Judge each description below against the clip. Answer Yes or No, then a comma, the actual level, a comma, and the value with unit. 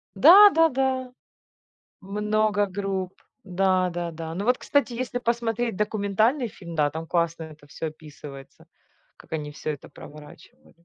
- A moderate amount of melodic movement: No, wide, 6.5 semitones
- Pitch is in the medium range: No, high, 195 Hz